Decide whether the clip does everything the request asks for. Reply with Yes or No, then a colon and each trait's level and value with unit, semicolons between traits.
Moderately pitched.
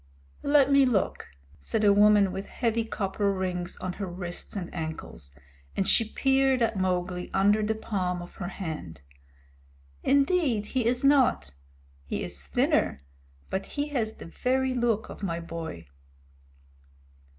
No: high, 205 Hz